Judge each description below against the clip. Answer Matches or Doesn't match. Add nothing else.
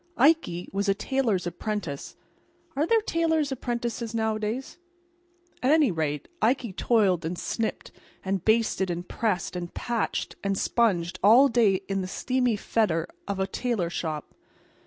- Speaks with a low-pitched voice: Doesn't match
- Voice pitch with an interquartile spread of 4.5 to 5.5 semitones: Matches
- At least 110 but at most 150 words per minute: Matches